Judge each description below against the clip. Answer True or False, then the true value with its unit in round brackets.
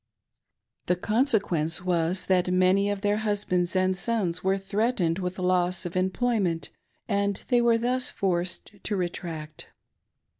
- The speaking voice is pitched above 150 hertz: True (185 Hz)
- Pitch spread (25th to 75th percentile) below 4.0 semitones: True (2.6 semitones)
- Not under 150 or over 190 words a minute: False (140 wpm)